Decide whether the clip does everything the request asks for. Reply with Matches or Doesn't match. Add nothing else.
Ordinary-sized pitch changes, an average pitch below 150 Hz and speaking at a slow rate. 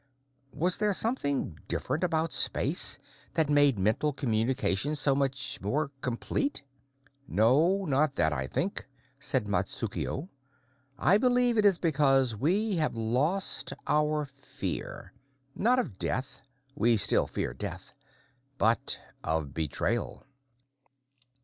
Doesn't match